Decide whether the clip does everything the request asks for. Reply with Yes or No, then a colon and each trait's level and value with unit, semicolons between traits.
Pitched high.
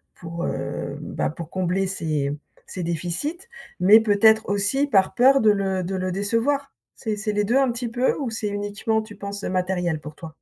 Yes: high, 200 Hz